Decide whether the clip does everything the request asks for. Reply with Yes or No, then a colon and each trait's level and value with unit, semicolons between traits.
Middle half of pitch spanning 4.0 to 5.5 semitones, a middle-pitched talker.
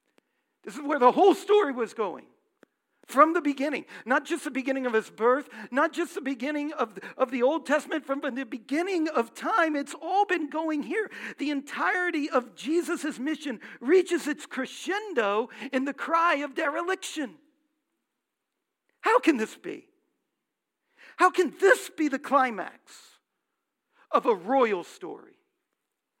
No: average, 4.4 semitones; very high, 300 Hz